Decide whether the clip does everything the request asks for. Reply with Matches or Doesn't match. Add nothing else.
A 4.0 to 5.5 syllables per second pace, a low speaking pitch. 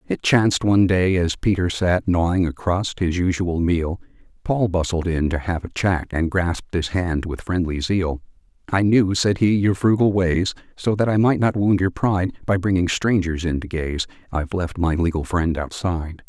Matches